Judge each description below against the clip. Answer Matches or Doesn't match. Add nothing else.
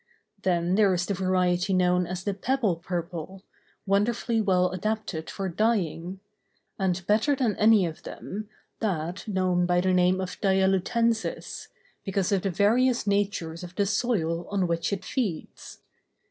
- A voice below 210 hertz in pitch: Matches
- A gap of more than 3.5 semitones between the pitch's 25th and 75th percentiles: Doesn't match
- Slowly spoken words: Doesn't match